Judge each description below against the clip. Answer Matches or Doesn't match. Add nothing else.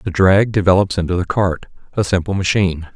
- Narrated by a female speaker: Doesn't match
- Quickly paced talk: Doesn't match